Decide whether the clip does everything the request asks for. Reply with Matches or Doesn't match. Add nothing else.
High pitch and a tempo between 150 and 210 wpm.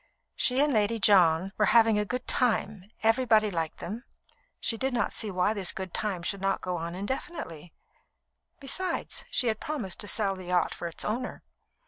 Matches